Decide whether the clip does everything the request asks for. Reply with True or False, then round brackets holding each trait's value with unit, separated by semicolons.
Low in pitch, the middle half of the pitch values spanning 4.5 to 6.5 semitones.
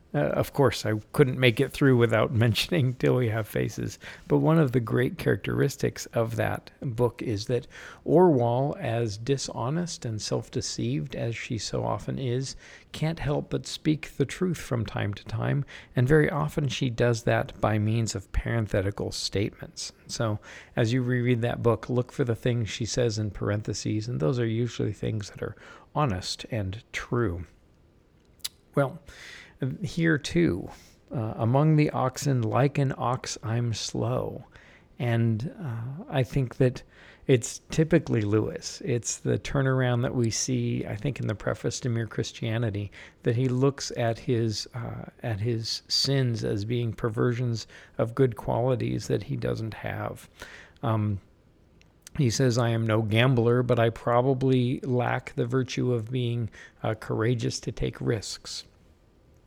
False (120 Hz; 3.1 semitones)